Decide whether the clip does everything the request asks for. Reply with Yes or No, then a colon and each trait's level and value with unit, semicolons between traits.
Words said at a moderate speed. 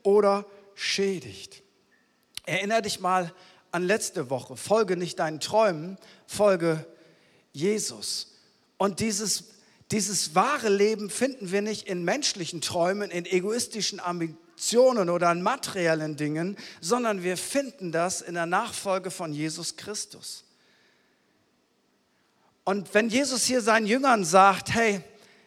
No: slow, 120 wpm